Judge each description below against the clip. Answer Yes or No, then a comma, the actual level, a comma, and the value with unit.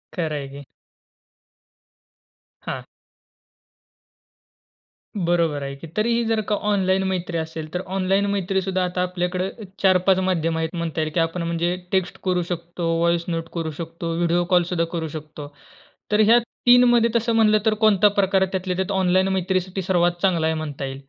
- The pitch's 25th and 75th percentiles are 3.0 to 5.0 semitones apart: No, narrow, 2.5 semitones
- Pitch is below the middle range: No, medium, 180 Hz